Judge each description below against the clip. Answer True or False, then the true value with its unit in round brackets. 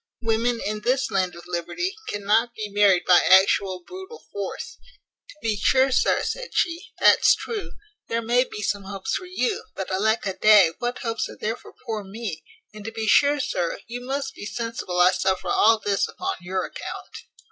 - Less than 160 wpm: False (190 wpm)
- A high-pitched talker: True (220 Hz)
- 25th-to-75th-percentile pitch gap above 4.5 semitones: False (4.2 semitones)